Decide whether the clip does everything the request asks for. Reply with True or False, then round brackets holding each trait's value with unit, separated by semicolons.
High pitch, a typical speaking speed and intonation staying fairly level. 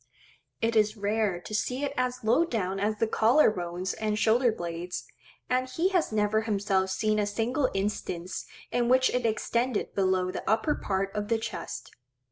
False (215 Hz; 175 wpm; 3.7 semitones)